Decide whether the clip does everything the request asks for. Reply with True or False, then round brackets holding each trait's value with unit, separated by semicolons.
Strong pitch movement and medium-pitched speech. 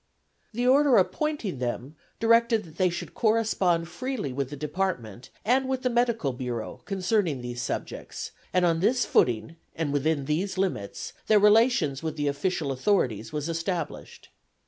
True (7.8 semitones; 175 Hz)